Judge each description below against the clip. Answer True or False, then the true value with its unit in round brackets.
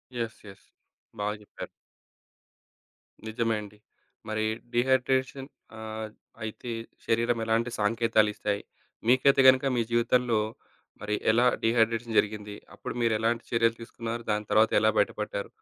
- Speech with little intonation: True (1.6 semitones)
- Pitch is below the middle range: True (115 Hz)